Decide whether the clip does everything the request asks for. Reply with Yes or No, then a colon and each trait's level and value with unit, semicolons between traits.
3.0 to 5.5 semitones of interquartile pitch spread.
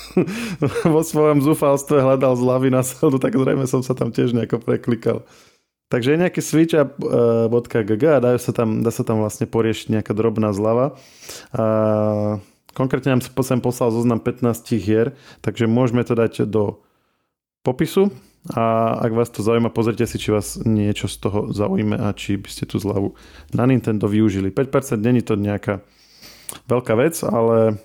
Yes: average, 3.4 semitones